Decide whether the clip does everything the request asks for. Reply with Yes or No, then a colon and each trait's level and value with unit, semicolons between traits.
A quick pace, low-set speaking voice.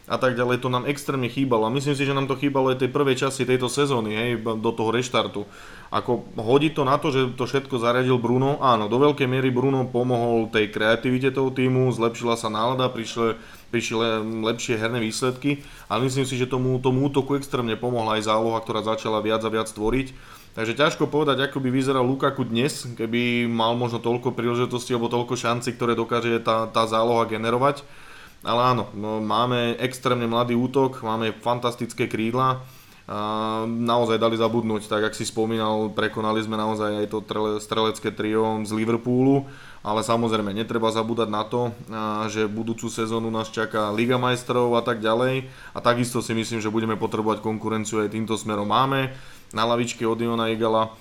Yes: fast, 175 wpm; low, 115 Hz